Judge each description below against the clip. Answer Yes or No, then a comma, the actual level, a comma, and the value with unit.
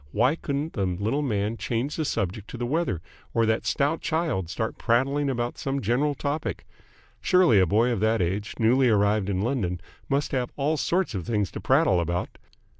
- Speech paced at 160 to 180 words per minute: No, average, 190 wpm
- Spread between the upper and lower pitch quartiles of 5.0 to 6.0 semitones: Yes, wide, 5.6 semitones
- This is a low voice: Yes, low, 120 Hz